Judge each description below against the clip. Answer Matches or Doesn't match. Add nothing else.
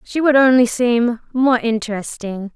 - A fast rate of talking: Doesn't match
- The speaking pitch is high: Matches